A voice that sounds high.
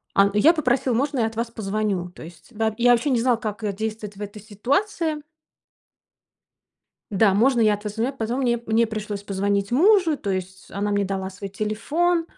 Yes: high, 220 Hz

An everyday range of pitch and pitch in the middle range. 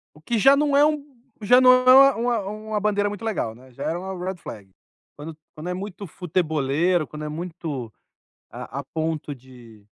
No: wide, 6.4 semitones; medium, 180 Hz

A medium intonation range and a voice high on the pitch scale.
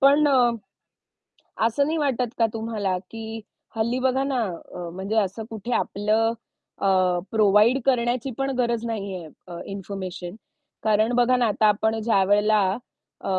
Yes: average, 3.4 semitones; high, 225 Hz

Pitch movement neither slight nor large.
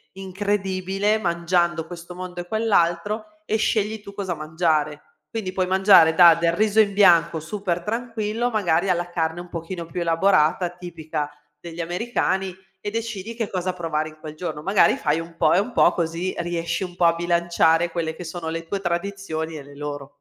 Yes: average, 3.2 semitones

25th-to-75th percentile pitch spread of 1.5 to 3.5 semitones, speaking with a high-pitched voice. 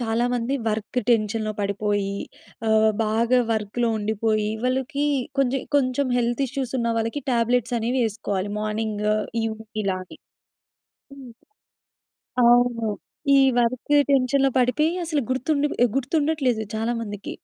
Yes: average, 3.0 semitones; high, 235 Hz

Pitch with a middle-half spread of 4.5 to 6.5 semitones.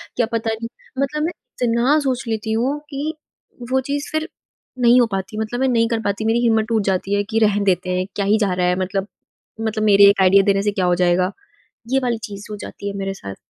No: average, 3.6 semitones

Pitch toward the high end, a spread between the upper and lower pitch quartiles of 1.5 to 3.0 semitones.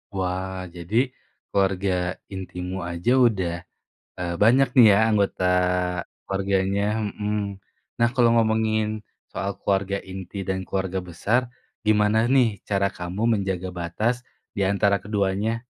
No: low, 100 Hz; narrow, 2.6 semitones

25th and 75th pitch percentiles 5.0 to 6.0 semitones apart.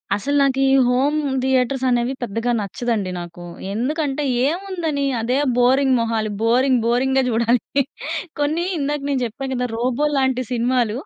No: average, 2.9 semitones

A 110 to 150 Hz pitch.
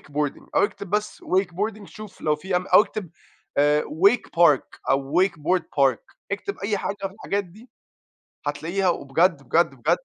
No: medium, 180 Hz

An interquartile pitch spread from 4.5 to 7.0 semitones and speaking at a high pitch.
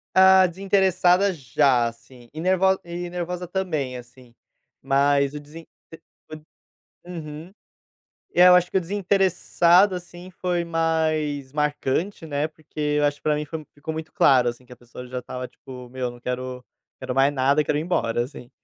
No: average, 5.2 semitones; medium, 155 Hz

